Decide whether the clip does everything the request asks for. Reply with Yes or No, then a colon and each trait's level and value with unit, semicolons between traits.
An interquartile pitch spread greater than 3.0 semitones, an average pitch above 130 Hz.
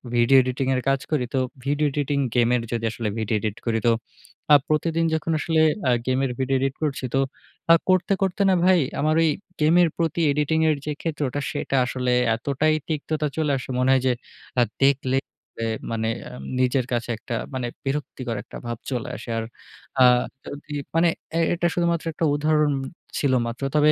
Yes: average, 3.7 semitones; medium, 140 Hz